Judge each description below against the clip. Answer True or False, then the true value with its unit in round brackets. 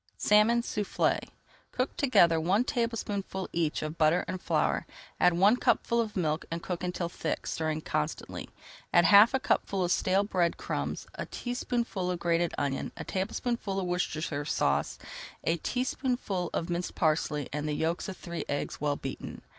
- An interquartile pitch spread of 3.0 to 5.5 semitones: True (4.4 semitones)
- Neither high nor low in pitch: True (180 Hz)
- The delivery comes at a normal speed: True (160 wpm)